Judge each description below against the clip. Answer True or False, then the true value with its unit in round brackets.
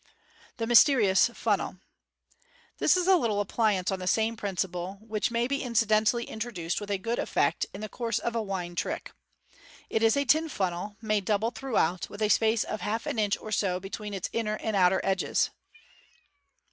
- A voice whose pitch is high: True (215 Hz)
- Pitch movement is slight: False (3.1 semitones)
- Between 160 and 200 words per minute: True (185 wpm)